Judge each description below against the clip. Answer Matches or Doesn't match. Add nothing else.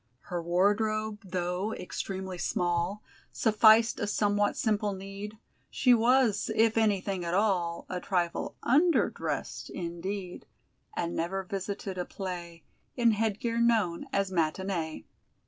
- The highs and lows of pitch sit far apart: Doesn't match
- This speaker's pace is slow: Matches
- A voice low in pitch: Doesn't match